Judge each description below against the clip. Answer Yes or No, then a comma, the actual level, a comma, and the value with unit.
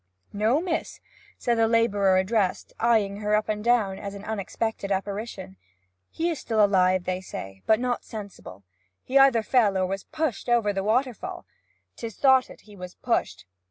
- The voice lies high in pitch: Yes, high, 215 Hz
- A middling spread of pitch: Yes, average, 3.5 semitones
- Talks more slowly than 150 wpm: No, average, 165 wpm